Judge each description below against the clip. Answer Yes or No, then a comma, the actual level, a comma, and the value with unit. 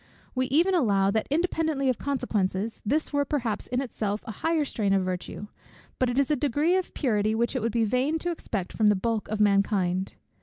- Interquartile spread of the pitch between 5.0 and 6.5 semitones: Yes, wide, 5.6 semitones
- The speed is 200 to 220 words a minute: Yes, fast, 205 wpm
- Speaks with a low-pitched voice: No, high, 235 Hz